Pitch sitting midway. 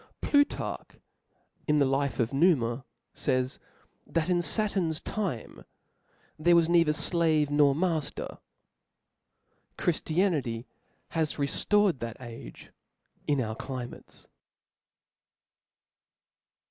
Yes: medium, 150 Hz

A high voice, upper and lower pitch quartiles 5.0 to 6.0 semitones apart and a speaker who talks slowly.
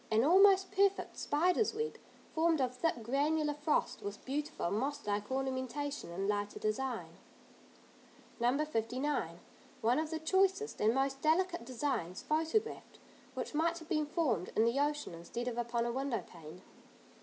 No: very high, 275 Hz; wide, 5.4 semitones; average, 145 wpm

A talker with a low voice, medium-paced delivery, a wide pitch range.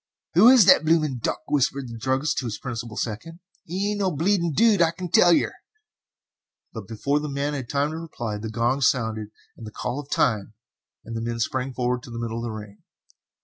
No: low, 130 Hz; fast, 210 wpm; wide, 5.8 semitones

